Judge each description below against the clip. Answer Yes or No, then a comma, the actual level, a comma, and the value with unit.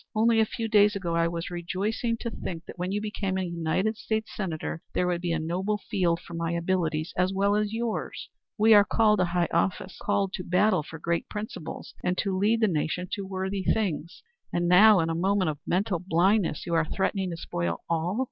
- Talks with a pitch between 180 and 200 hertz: Yes, medium, 185 Hz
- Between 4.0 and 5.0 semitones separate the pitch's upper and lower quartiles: No, average, 3.5 semitones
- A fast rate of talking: Yes, fast, 215 wpm